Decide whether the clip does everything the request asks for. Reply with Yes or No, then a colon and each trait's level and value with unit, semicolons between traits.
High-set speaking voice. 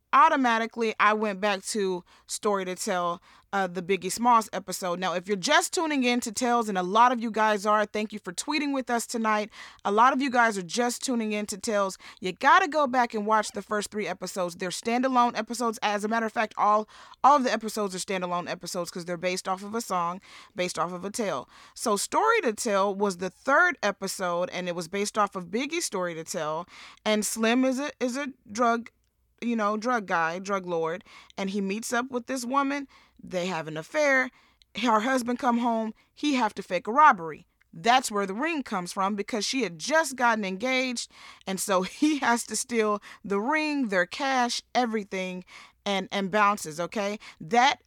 Yes: high, 215 Hz